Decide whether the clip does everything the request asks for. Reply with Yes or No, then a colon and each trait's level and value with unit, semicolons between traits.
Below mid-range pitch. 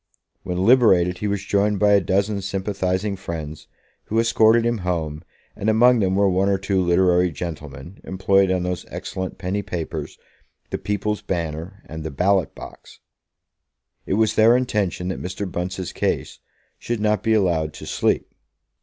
Yes: very low, 95 Hz